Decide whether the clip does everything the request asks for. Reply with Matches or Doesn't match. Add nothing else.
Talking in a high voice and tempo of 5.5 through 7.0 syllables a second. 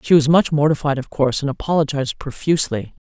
Doesn't match